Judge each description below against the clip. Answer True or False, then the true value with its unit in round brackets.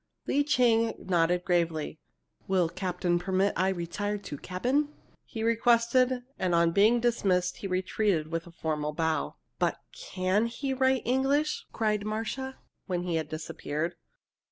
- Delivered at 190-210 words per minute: False (140 wpm)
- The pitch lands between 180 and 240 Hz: True (190 Hz)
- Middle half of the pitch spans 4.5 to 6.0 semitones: True (5.6 semitones)